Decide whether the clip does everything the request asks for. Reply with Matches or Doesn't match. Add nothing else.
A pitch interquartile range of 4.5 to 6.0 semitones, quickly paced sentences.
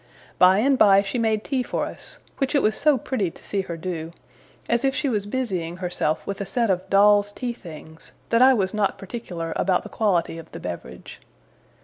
Matches